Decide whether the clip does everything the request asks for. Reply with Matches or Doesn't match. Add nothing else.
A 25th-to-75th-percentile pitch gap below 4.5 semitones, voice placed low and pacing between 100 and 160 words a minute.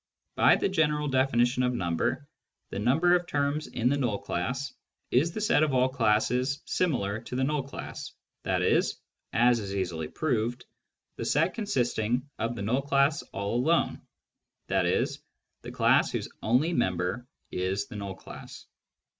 Doesn't match